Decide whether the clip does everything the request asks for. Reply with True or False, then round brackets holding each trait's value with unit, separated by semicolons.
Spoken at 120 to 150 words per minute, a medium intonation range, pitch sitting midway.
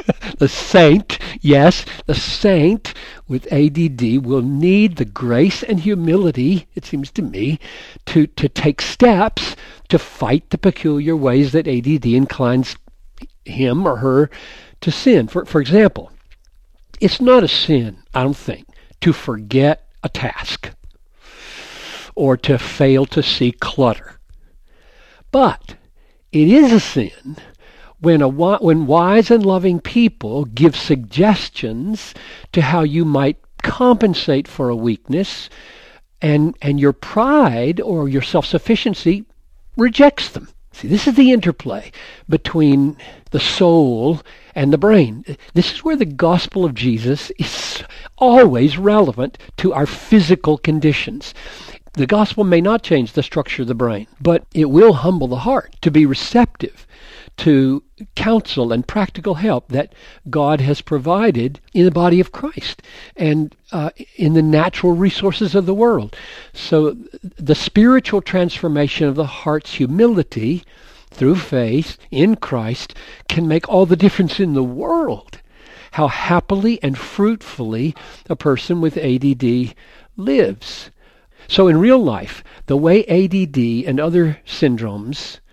False (140 wpm; 5.7 semitones; 160 Hz)